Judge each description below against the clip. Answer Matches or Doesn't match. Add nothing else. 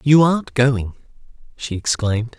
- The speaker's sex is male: Matches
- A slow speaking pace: Matches